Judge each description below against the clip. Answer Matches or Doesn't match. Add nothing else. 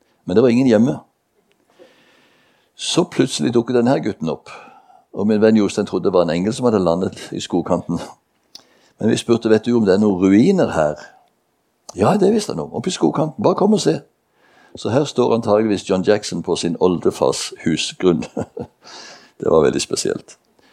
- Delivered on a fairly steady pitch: Matches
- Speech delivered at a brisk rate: Doesn't match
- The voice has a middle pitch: Doesn't match